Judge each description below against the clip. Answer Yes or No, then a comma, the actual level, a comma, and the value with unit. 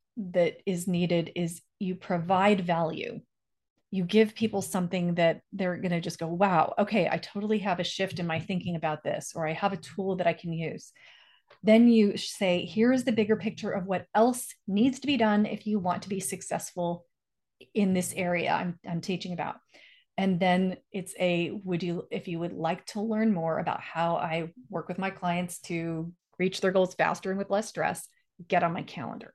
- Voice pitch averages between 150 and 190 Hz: Yes, medium, 185 Hz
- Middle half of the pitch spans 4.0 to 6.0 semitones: No, average, 3.0 semitones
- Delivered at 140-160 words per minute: No, average, 200 wpm